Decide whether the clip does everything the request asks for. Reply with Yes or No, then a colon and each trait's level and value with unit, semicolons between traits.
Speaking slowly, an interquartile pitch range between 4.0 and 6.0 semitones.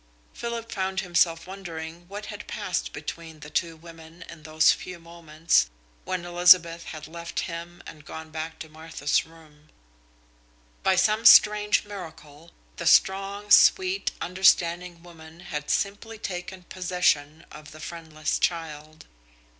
No: slow, 130 wpm; average, 2.7 semitones